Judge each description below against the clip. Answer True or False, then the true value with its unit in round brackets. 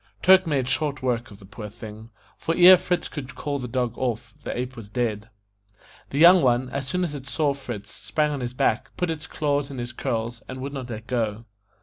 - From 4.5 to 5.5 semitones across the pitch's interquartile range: False (4.0 semitones)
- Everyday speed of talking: False (225 wpm)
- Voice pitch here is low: True (130 Hz)